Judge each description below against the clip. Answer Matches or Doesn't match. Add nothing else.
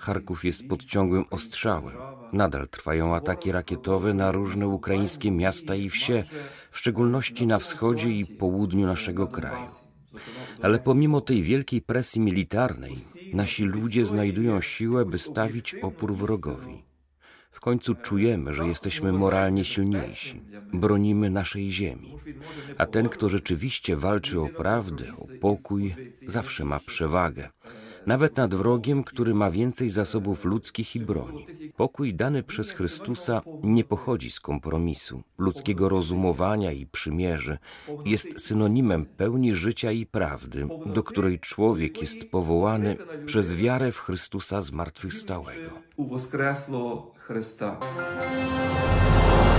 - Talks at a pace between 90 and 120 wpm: Matches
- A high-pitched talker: Doesn't match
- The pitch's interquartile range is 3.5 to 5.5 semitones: Matches